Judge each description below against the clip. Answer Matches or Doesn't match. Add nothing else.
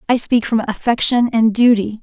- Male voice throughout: Doesn't match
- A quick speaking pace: Doesn't match